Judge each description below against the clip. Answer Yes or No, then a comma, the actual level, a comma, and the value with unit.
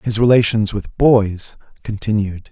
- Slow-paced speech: Yes, slow, 120 wpm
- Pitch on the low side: Yes, low, 105 Hz